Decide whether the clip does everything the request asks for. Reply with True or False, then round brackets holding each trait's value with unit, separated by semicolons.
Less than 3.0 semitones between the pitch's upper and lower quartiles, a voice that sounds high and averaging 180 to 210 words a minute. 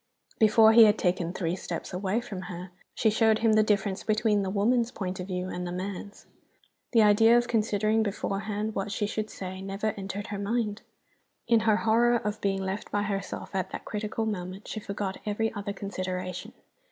True (2.4 semitones; 205 Hz; 190 wpm)